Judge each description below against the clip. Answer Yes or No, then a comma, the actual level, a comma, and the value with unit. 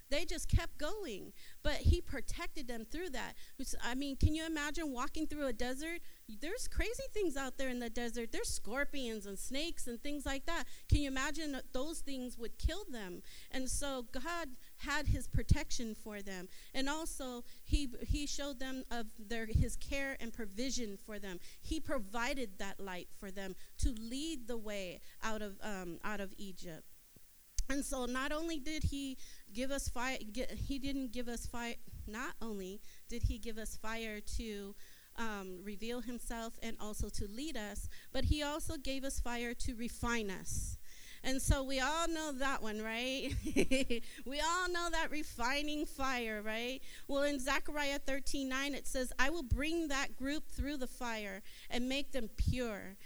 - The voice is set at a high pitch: Yes, very high, 260 Hz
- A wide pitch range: No, average, 4.0 semitones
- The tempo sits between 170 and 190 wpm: Yes, average, 180 wpm